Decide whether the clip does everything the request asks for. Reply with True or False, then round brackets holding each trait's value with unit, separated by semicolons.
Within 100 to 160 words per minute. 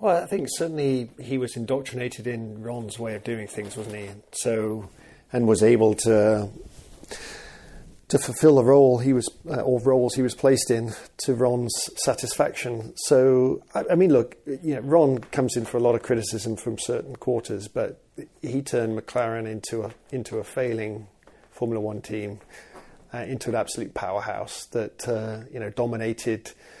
False (170 wpm)